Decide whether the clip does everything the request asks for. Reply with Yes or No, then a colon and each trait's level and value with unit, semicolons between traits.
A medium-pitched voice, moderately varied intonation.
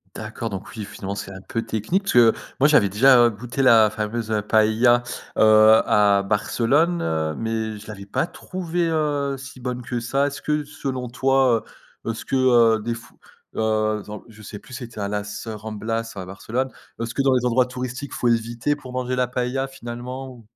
No: low, 115 Hz; average, 3.2 semitones